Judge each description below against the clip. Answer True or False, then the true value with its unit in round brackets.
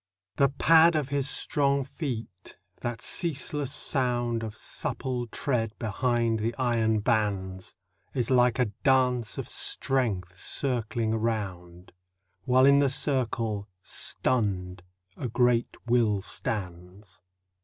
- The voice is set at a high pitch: False (120 Hz)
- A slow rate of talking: True (110 wpm)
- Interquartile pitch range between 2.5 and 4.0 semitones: True (3.7 semitones)